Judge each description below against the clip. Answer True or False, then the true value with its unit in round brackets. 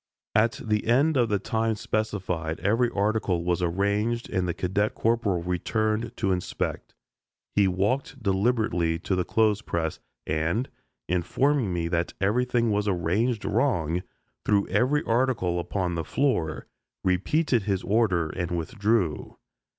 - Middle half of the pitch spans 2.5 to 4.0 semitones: False (4.6 semitones)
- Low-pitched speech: True (100 Hz)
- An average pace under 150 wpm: True (135 wpm)